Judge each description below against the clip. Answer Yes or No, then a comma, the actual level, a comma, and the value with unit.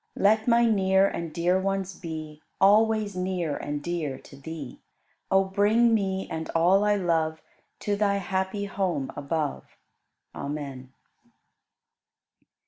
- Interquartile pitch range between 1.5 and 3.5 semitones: No, average, 4.1 semitones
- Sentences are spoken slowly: Yes, slow, 125 wpm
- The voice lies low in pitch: No, high, 190 Hz